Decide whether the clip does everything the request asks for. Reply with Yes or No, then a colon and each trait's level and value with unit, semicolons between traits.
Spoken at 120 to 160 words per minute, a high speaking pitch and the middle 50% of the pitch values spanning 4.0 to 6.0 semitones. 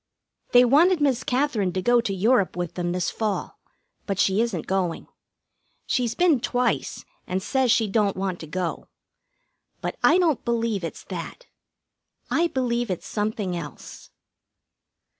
Yes: average, 145 wpm; high, 220 Hz; average, 5.1 semitones